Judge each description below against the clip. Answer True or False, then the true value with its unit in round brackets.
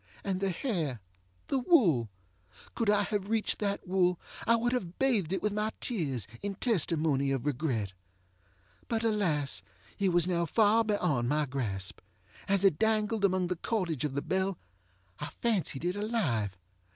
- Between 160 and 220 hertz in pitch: True (185 Hz)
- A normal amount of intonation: False (6.6 semitones)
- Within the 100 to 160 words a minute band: True (155 wpm)